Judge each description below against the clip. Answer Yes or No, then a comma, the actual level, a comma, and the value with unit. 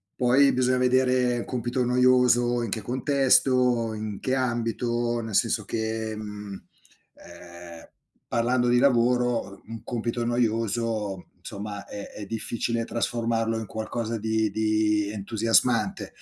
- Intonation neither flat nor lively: No, narrow, 2.2 semitones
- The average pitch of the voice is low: Yes, low, 115 Hz